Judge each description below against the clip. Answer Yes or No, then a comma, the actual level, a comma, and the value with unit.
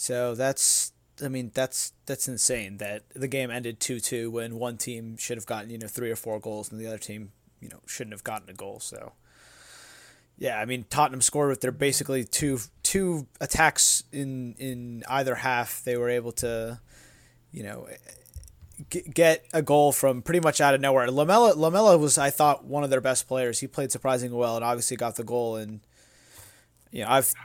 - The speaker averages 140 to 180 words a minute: No, average, 195 wpm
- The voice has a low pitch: Yes, low, 125 Hz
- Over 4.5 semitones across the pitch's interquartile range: No, average, 3.0 semitones